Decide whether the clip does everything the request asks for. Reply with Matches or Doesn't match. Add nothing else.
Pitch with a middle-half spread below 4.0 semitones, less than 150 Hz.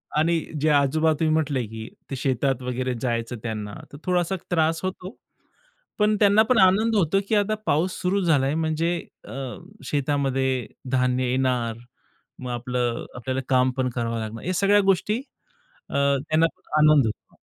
Doesn't match